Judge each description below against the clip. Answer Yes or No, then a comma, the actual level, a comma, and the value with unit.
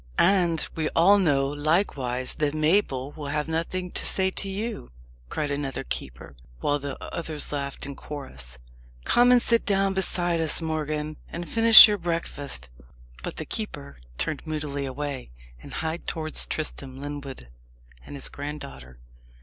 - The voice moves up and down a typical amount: Yes, average, 3.7 semitones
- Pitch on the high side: No, medium, 150 Hz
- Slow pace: No, average, 150 wpm